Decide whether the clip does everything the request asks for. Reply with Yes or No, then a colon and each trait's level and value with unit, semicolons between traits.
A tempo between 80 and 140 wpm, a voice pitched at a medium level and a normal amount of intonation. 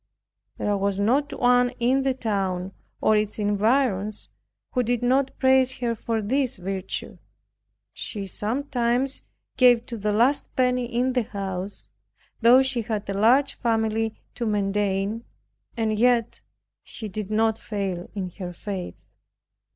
No: slow, 135 wpm; high, 225 Hz; average, 3.5 semitones